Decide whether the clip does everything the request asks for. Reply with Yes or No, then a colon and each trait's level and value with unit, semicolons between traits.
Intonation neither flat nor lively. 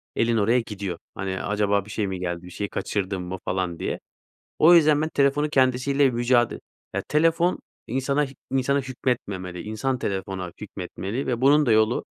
No: wide, 6.0 semitones